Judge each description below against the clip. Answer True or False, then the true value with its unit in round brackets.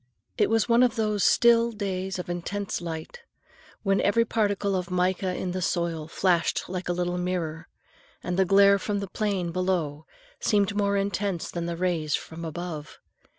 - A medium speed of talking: True (170 wpm)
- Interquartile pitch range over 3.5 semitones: False (2.7 semitones)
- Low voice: False (185 Hz)